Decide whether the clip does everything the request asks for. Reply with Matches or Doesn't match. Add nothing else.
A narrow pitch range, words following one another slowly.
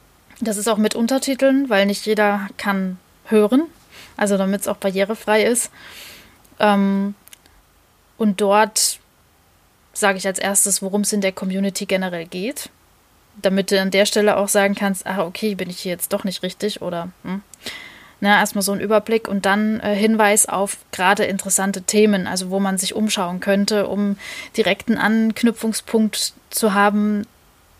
Doesn't match